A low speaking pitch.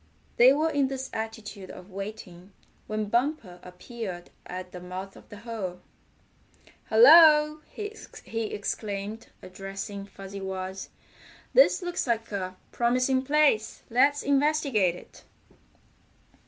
No: high, 220 Hz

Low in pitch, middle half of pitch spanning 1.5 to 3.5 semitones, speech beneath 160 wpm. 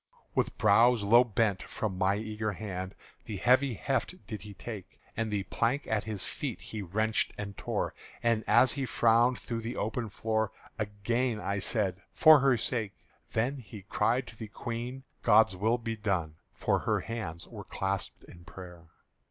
No: low, 110 Hz; average, 2.9 semitones; average, 170 wpm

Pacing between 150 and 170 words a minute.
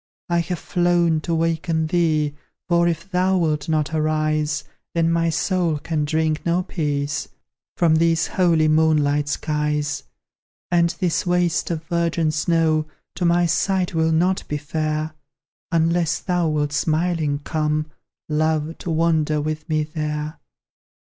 No: slow, 135 wpm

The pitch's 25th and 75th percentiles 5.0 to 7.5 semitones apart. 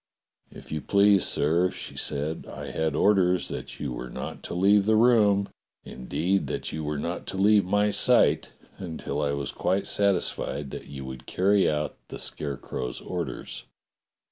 Yes: wide, 5.6 semitones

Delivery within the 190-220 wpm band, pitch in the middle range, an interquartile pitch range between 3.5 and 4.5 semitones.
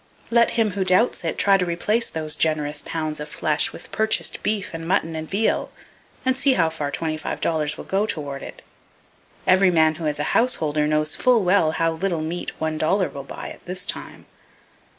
Yes: average, 200 wpm; medium, 165 Hz; average, 4.1 semitones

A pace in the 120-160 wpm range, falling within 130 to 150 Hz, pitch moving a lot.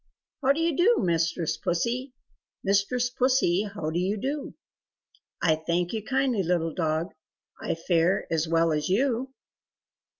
No: average, 140 wpm; high, 195 Hz; wide, 7.3 semitones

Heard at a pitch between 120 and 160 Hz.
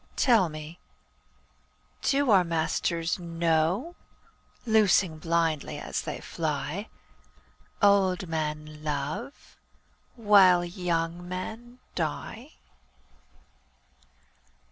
No: medium, 170 Hz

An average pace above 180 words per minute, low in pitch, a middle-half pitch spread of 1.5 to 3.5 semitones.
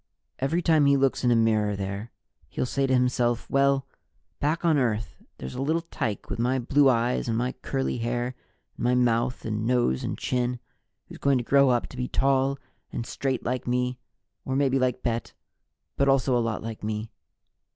Yes: average, 195 wpm; low, 125 Hz; average, 2.7 semitones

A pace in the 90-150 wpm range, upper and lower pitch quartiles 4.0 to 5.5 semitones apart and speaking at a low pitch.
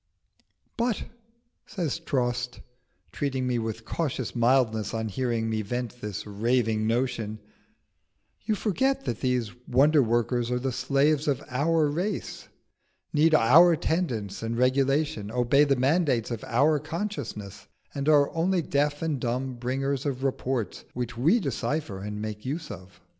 Yes: average, 140 wpm; average, 4.4 semitones; low, 130 Hz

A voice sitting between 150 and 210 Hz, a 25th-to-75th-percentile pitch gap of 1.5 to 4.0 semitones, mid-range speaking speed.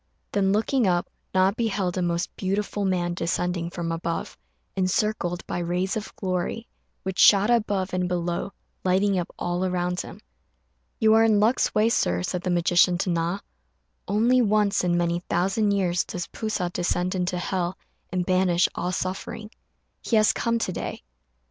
Yes: medium, 185 Hz; average, 2.7 semitones; average, 165 wpm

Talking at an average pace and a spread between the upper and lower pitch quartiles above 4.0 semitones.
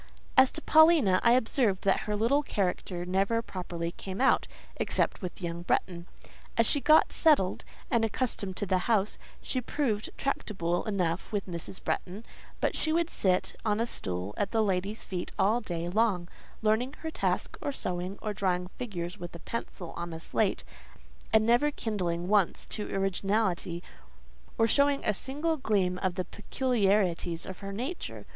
Yes: average, 165 wpm; average, 4.5 semitones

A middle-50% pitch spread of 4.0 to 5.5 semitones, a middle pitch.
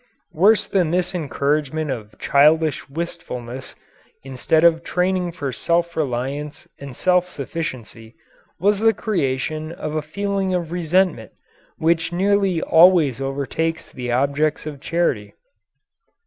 Yes: average, 4.3 semitones; medium, 160 Hz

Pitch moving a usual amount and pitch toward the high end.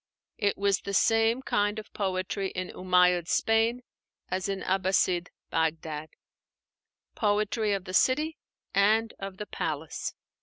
Yes: average, 3.0 semitones; high, 195 Hz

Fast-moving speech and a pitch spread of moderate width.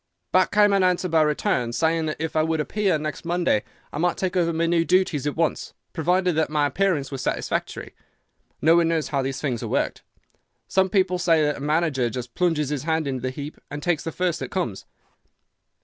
Yes: fast, 210 wpm; average, 3.3 semitones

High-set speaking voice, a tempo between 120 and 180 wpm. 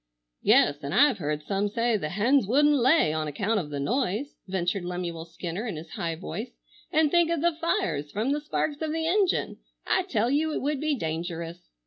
No: high, 210 Hz; average, 200 wpm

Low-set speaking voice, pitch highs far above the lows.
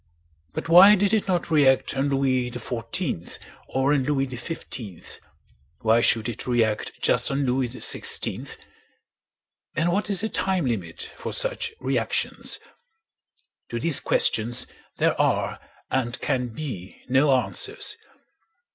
Yes: low, 130 Hz; wide, 6.1 semitones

